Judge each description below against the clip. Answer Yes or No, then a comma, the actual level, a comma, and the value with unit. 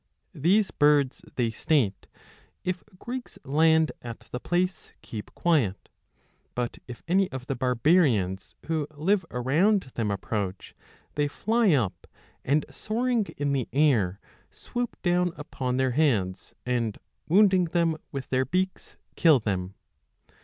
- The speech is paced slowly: Yes, slow, 130 wpm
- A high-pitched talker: No, medium, 145 Hz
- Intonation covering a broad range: Yes, wide, 6.6 semitones